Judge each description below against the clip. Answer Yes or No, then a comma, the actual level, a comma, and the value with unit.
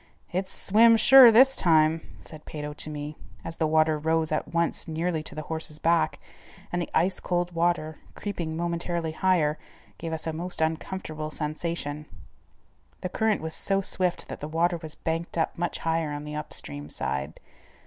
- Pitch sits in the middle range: Yes, medium, 160 Hz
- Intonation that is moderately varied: No, narrow, 2.2 semitones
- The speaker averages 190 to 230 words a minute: No, average, 170 wpm